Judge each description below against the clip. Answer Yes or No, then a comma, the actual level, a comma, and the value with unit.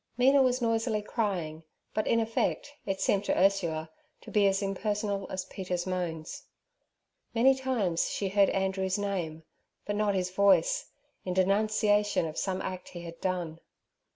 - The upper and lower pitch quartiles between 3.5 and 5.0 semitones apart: No, average, 2.7 semitones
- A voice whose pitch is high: Yes, high, 195 Hz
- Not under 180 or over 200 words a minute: No, average, 155 wpm